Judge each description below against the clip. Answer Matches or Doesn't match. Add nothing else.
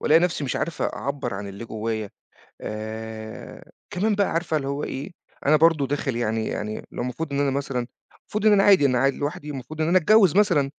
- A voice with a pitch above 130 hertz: Matches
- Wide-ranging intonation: Matches